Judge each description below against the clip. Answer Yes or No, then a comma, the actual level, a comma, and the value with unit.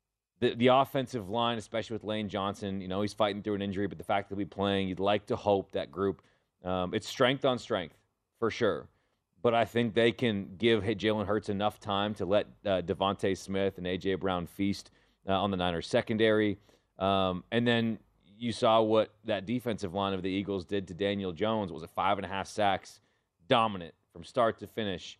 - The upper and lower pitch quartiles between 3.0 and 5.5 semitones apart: No, narrow, 2.5 semitones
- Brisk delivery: Yes, fast, 210 wpm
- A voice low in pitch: Yes, low, 100 Hz